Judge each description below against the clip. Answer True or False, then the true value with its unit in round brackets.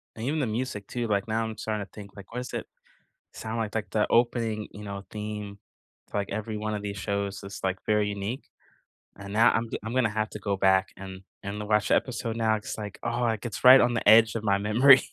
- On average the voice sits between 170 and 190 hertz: False (105 Hz)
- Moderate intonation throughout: False (2.2 semitones)